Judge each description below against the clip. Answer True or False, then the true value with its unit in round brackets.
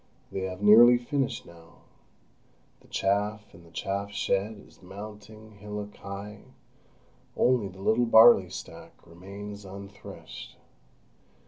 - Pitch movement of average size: False (1.9 semitones)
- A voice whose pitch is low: True (100 Hz)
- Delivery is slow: True (115 wpm)